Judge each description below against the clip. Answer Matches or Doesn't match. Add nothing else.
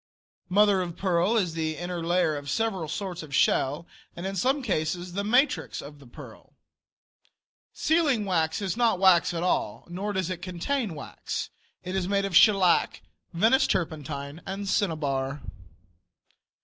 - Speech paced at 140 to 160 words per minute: Matches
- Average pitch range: Matches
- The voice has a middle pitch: Matches